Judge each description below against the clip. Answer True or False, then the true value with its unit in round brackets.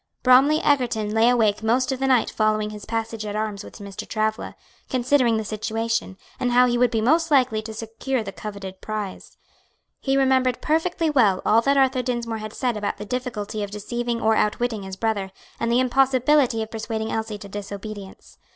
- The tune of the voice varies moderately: True (3.0 semitones)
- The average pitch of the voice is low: False (225 Hz)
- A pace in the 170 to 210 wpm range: True (190 wpm)